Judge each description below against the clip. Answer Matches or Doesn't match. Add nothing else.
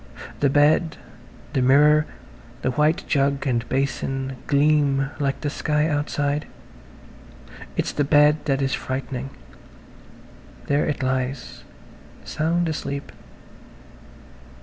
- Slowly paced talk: Matches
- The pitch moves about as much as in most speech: Doesn't match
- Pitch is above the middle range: Doesn't match